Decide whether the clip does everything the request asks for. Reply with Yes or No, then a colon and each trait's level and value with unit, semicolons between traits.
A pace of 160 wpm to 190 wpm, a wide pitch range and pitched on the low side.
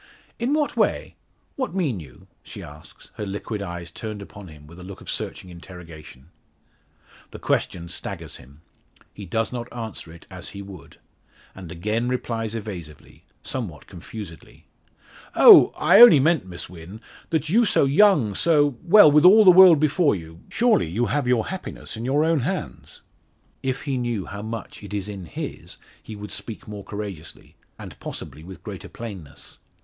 Yes: average, 165 wpm; wide, 8.1 semitones; low, 105 Hz